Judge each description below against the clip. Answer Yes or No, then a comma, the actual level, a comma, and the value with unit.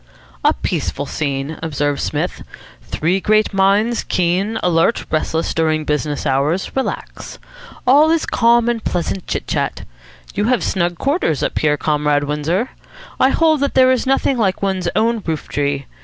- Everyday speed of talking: Yes, average, 155 wpm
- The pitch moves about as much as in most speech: No, wide, 7.5 semitones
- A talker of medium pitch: Yes, medium, 180 Hz